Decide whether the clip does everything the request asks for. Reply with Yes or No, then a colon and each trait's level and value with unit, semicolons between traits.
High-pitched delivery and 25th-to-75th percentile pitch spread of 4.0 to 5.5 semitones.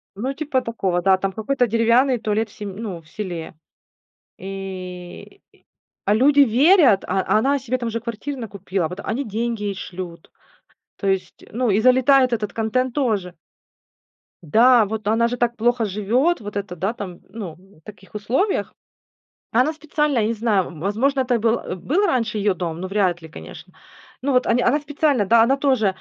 Yes: high, 220 Hz; average, 4.7 semitones